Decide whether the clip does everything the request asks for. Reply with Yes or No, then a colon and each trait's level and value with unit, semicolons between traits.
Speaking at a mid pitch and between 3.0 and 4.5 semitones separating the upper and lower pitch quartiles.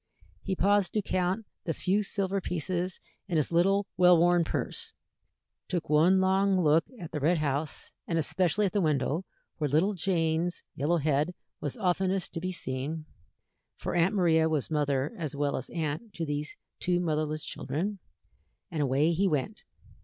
Yes: medium, 170 Hz; average, 3.6 semitones